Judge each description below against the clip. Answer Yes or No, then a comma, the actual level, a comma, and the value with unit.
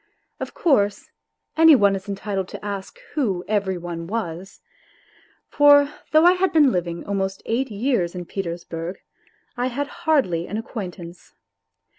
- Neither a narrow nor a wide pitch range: No, wide, 7.4 semitones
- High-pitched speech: Yes, high, 200 Hz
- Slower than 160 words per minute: Yes, average, 140 wpm